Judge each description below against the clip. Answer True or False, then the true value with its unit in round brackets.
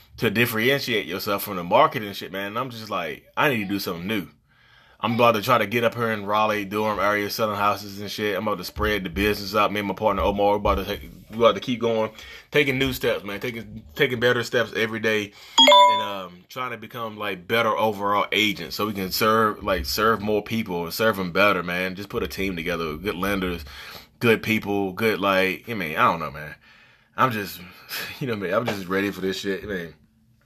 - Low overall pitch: True (105 Hz)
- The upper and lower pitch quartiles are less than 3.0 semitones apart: True (2.5 semitones)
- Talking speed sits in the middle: False (235 wpm)